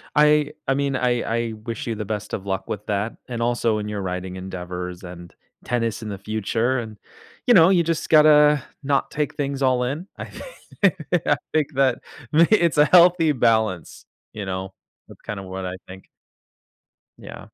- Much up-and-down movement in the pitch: Yes, wide, 7.1 semitones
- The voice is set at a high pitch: No, low, 115 Hz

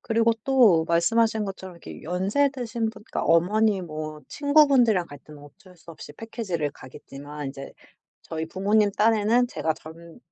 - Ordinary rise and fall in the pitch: No, wide, 5.9 semitones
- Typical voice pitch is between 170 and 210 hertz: Yes, high, 190 Hz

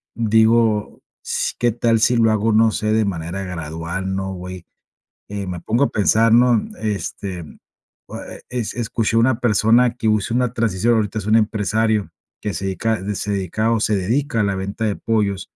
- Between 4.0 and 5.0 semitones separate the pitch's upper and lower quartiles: No, average, 2.8 semitones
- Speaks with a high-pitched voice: No, low, 110 Hz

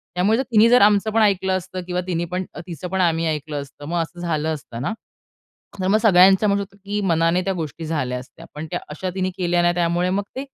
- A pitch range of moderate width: Yes, average, 3.2 semitones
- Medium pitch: Yes, medium, 180 Hz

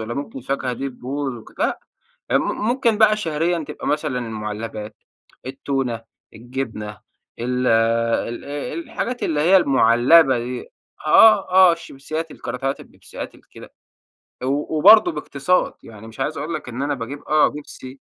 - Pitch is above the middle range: No, low, 135 Hz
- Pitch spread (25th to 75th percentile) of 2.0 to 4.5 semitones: No, average, 5.1 semitones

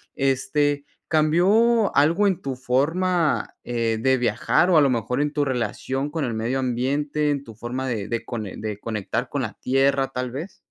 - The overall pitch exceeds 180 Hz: No, low, 135 Hz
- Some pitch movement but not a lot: Yes, average, 3.7 semitones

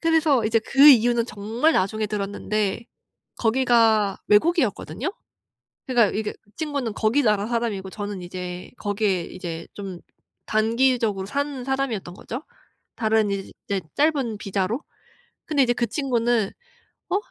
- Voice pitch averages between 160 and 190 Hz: No, high, 220 Hz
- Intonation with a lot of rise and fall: No, average, 4.2 semitones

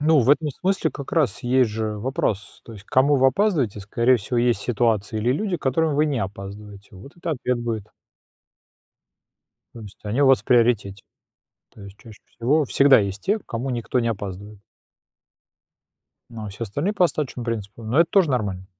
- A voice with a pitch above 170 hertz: No, low, 120 Hz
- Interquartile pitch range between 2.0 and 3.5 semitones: No, average, 5.1 semitones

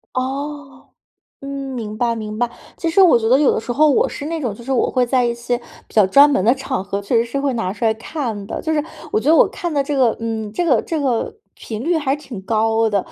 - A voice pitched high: Yes, very high, 250 Hz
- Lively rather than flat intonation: No, average, 4.2 semitones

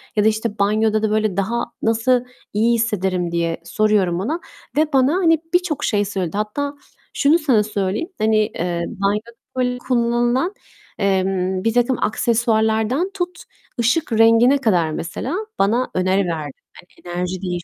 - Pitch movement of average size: Yes, average, 4.5 semitones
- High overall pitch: Yes, high, 220 Hz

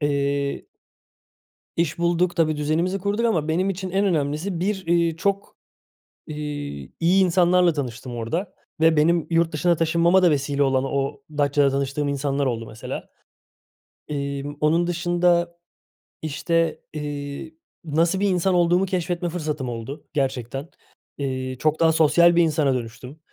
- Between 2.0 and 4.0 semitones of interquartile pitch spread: Yes, average, 3.6 semitones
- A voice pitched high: No, medium, 155 Hz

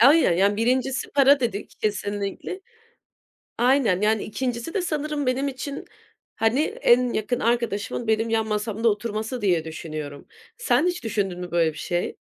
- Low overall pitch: No, high, 225 Hz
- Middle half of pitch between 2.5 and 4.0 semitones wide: No, average, 4.4 semitones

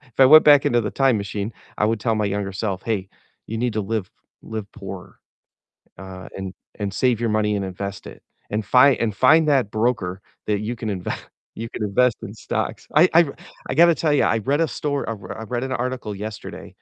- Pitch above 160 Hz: No, low, 110 Hz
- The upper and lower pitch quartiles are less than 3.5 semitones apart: No, average, 4.1 semitones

